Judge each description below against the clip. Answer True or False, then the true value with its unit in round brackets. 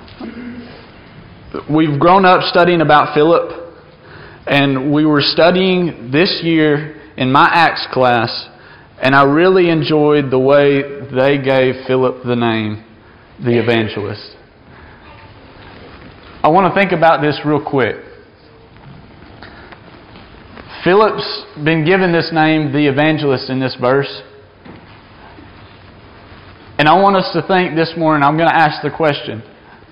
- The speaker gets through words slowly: True (120 wpm)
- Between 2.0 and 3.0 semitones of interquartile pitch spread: False (5.2 semitones)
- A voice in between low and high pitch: True (145 Hz)